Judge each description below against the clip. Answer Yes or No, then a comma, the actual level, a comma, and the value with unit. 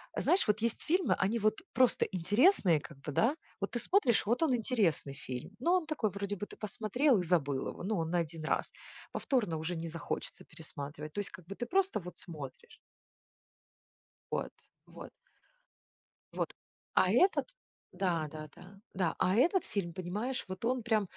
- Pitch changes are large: Yes, wide, 6.5 semitones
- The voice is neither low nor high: No, high, 195 Hz